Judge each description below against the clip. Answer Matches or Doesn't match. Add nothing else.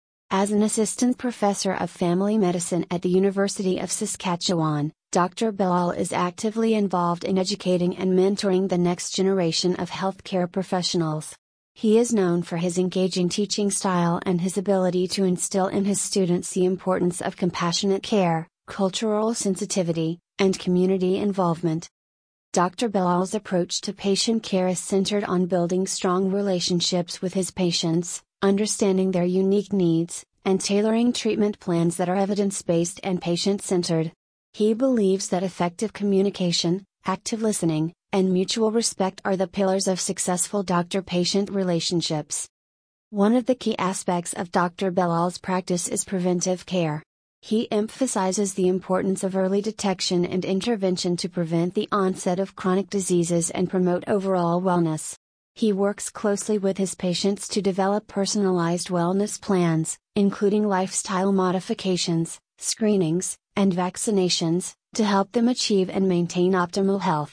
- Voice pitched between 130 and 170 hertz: Doesn't match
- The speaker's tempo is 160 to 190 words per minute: Doesn't match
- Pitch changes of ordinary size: Doesn't match